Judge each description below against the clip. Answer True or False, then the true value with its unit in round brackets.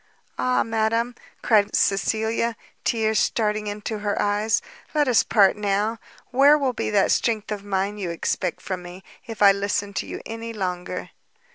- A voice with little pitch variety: True (2.2 semitones)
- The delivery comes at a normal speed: True (160 wpm)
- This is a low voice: False (210 Hz)